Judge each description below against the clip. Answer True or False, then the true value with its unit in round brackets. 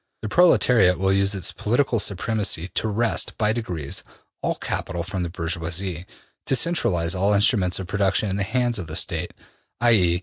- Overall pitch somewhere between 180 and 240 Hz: False (100 Hz)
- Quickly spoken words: False (170 wpm)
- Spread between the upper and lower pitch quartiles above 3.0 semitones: True (3.8 semitones)